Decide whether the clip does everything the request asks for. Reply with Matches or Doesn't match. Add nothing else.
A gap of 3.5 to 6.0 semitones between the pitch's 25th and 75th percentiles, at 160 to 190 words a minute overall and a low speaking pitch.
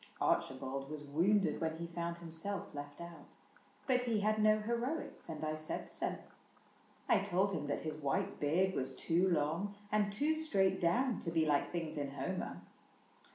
Doesn't match